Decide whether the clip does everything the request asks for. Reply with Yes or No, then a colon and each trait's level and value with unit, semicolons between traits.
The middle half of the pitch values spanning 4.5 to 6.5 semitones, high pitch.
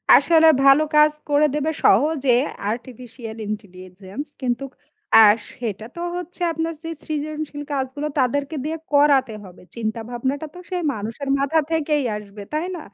Yes: average, 5.3 semitones; very high, 275 Hz